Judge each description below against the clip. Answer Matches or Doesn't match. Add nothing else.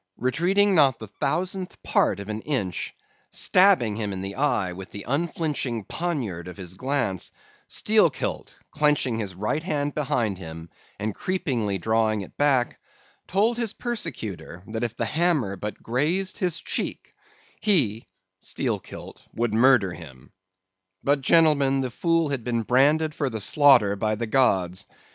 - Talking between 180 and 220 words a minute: Doesn't match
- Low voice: Matches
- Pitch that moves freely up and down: Matches